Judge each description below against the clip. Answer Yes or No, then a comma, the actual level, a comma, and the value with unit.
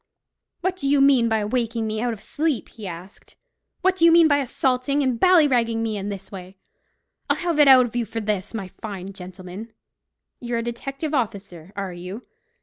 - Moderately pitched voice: No, high, 230 Hz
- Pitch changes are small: No, wide, 5.5 semitones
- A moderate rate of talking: Yes, average, 195 wpm